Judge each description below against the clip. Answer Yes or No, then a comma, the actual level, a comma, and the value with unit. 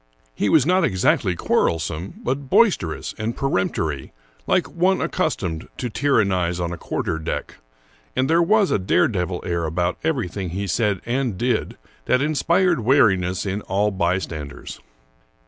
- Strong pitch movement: Yes, wide, 7.7 semitones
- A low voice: Yes, low, 100 Hz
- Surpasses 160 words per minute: No, average, 150 wpm